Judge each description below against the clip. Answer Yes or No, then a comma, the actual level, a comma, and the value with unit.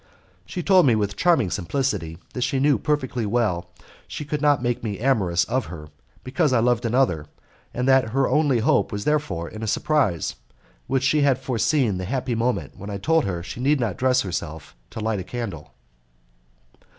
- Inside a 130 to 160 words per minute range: No, average, 195 wpm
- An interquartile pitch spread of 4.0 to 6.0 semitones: Yes, wide, 5.5 semitones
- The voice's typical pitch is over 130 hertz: No, low, 120 Hz